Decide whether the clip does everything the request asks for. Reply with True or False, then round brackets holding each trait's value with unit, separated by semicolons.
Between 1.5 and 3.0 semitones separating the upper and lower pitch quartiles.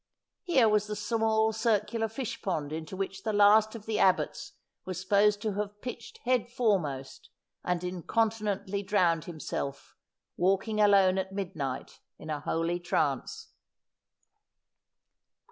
False (3.7 semitones)